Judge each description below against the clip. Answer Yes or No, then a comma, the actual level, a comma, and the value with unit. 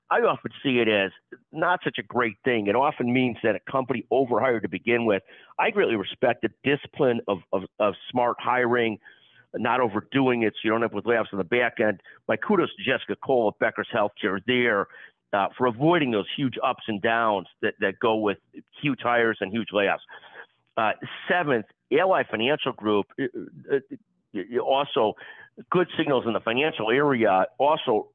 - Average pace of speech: Yes, average, 175 wpm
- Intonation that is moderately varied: Yes, average, 3.6 semitones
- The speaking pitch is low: Yes, low, 120 Hz